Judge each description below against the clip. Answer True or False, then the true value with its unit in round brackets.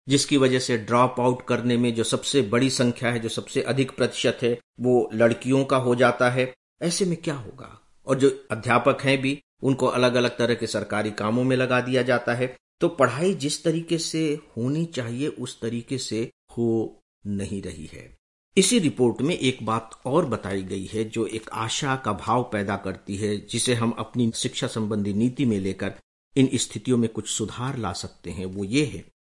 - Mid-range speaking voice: False (120 Hz)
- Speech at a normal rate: True (195 wpm)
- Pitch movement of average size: True (3.3 semitones)